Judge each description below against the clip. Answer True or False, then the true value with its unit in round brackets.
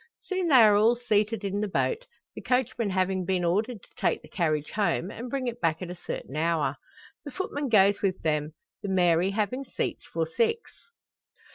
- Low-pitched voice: False (205 Hz)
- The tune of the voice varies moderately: False (5.7 semitones)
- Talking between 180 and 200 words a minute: True (190 wpm)